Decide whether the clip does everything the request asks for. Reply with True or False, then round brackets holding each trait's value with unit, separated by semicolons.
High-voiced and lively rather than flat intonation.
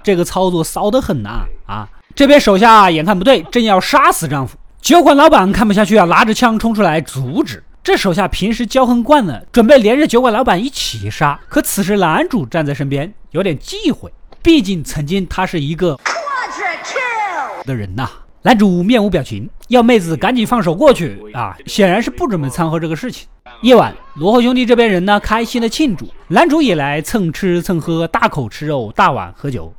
True (200 Hz; 8.1 semitones)